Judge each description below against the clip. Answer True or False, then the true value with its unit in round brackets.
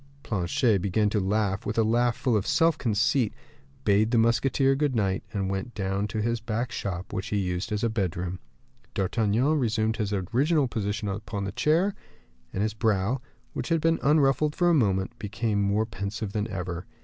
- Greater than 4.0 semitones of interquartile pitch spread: False (3.5 semitones)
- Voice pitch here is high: False (110 Hz)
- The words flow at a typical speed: True (185 wpm)